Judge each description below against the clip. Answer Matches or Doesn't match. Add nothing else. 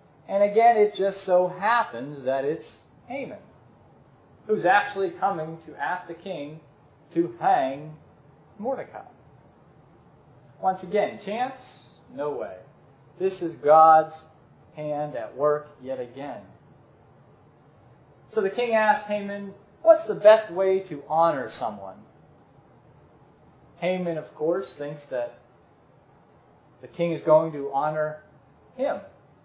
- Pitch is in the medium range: Matches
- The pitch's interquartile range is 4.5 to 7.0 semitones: Matches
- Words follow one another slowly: Matches